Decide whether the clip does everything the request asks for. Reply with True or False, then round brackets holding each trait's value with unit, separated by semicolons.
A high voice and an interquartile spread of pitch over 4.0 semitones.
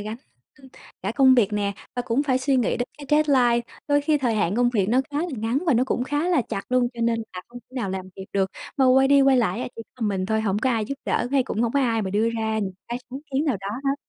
False (240 Hz; 3.7 semitones)